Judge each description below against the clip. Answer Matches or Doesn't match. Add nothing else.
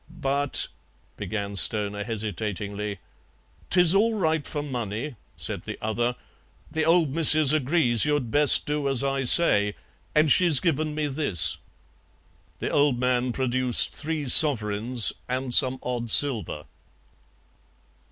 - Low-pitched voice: Matches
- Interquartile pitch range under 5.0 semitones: Doesn't match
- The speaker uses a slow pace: Matches